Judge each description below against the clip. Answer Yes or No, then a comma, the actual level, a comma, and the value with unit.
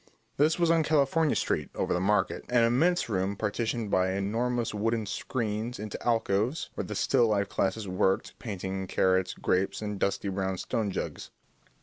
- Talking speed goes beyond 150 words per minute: Yes, average, 160 wpm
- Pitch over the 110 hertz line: No, low, 105 Hz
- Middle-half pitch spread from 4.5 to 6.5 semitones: No, average, 3.9 semitones